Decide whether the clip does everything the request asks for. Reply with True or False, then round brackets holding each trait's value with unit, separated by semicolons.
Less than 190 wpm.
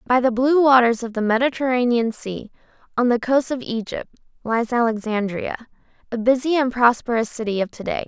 True (170 wpm)